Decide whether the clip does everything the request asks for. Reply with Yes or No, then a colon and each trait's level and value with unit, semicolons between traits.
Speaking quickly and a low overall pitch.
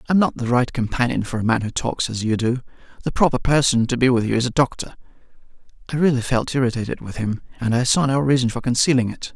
Yes: fast, 235 wpm; low, 125 Hz